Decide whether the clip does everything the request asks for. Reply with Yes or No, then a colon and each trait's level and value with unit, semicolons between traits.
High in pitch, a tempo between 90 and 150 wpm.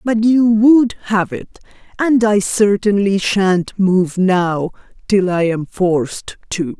Yes: high, 200 Hz; average, 140 wpm